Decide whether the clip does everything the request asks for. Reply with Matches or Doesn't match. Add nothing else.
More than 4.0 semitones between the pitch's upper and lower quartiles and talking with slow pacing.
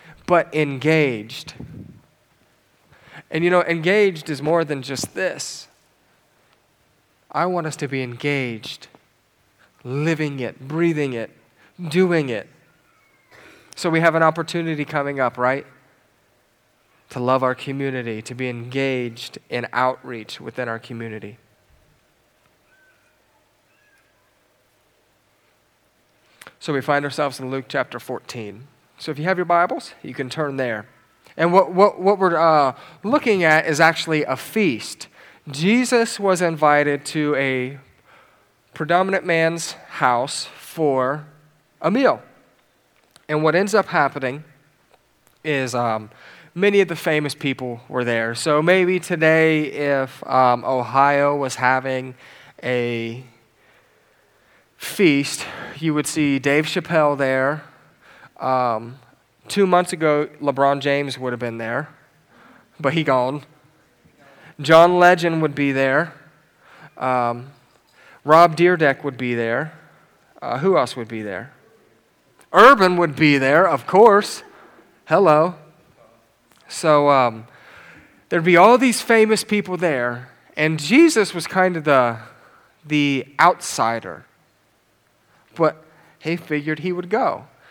Matches